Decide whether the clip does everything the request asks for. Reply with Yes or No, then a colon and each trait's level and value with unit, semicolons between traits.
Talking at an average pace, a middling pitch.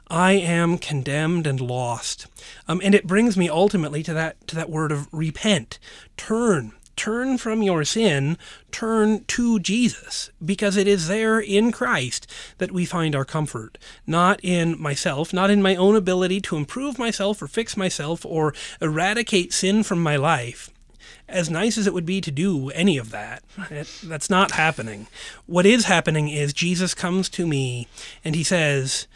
Yes: average, 170 wpm; medium, 175 Hz